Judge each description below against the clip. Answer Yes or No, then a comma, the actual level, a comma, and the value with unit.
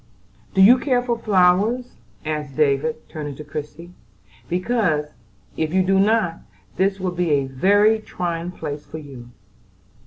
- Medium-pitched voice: Yes, medium, 180 Hz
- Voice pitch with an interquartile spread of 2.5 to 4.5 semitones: No, average, 5.3 semitones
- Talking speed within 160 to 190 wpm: No, average, 145 wpm